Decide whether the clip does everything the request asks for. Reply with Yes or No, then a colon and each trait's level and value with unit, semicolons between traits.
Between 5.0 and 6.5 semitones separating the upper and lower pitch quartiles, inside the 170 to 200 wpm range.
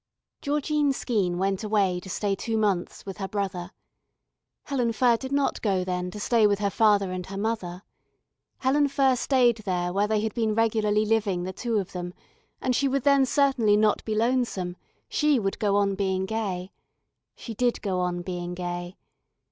No: average, 4.1 semitones; average, 180 wpm